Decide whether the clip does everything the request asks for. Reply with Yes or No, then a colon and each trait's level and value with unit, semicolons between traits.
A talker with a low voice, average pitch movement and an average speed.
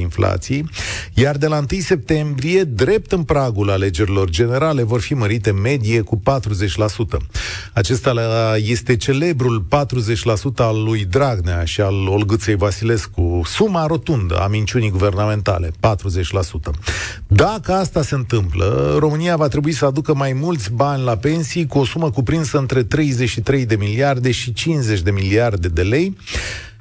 No: low, 115 Hz; wide, 6.0 semitones; average, 140 wpm